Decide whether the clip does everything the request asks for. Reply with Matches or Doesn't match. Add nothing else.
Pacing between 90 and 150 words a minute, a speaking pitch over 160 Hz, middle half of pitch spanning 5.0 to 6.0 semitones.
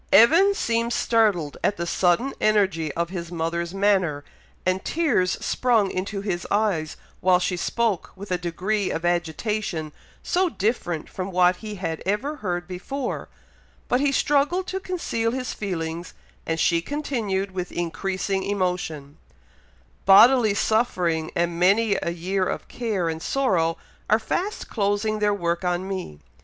Doesn't match